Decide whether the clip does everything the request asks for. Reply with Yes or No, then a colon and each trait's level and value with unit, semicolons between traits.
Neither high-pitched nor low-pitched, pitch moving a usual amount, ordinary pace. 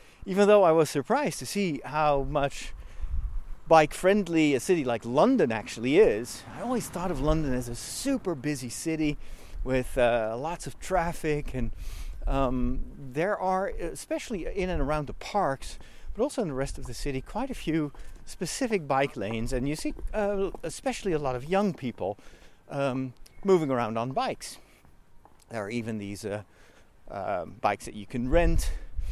No: medium, 145 Hz; wide, 7.6 semitones; average, 170 wpm